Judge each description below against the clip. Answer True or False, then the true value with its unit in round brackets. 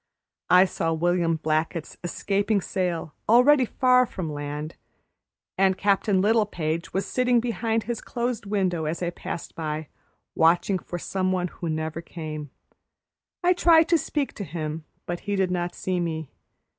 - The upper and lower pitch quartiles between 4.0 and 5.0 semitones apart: True (4.7 semitones)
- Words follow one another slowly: False (150 wpm)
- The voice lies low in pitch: False (180 Hz)